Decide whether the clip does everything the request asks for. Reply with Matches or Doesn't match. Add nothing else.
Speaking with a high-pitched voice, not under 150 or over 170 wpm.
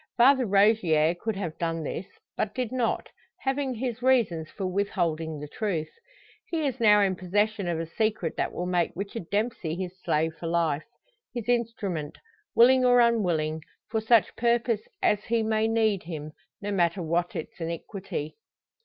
Matches